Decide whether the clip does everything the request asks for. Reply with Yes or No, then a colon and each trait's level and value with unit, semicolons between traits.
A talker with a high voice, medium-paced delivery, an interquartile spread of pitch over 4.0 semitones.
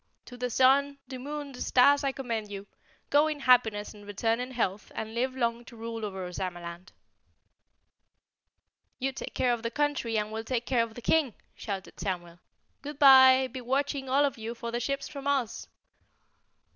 No: high, 245 Hz; average, 185 wpm; average, 3.5 semitones